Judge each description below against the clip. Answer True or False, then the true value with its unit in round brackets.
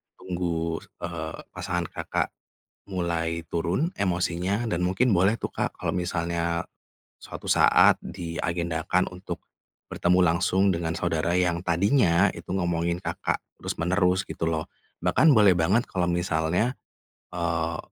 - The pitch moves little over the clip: True (1.9 semitones)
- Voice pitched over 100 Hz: False (90 Hz)